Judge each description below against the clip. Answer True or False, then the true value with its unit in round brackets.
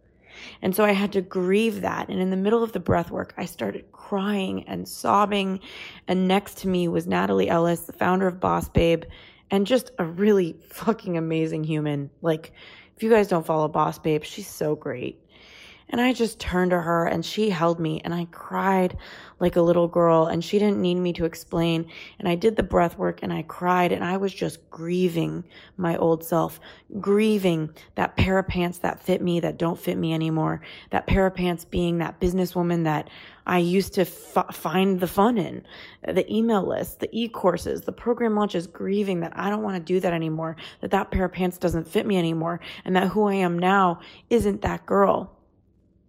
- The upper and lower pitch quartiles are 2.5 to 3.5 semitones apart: True (2.9 semitones)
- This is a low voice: False (180 Hz)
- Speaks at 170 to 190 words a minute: False (200 wpm)